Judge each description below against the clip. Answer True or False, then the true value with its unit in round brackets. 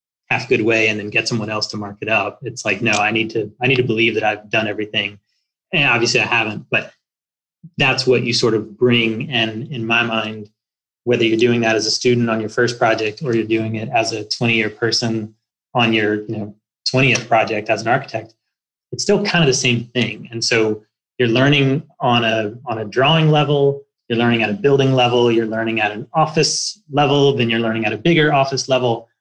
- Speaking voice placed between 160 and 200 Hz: False (115 Hz)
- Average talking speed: False (220 wpm)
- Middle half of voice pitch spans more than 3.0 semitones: False (2.7 semitones)